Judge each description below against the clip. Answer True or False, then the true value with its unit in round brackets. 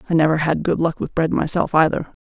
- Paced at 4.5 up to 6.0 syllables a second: False (6.2 syllables/s)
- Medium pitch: True (160 Hz)